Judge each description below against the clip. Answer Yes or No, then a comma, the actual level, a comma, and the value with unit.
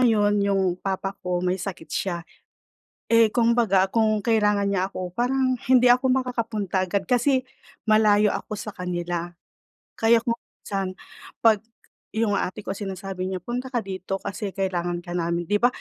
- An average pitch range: Yes, average, 3.7 semitones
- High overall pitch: Yes, high, 200 Hz